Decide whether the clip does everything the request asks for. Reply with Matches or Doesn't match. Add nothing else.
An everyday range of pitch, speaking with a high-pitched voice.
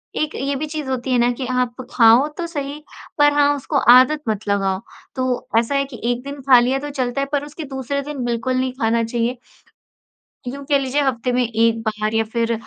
Matches